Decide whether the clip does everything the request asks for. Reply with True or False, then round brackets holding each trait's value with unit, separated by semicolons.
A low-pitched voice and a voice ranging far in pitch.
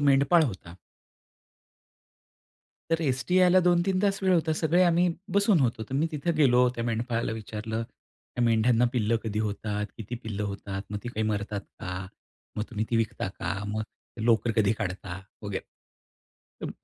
True (115 Hz; 7.0 semitones)